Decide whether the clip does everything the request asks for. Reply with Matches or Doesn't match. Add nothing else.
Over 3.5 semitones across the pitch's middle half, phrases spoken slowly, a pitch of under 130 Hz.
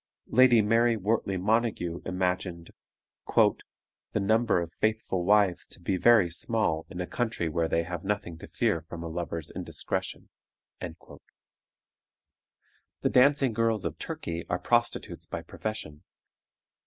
Matches